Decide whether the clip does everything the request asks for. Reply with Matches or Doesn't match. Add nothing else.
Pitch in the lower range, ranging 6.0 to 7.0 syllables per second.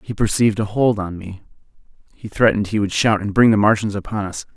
Matches